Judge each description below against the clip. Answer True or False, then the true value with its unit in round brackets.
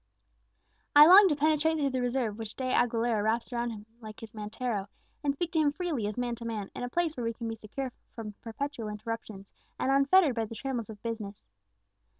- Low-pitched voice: False (235 Hz)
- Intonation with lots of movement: False (4.2 semitones)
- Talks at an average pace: False (210 wpm)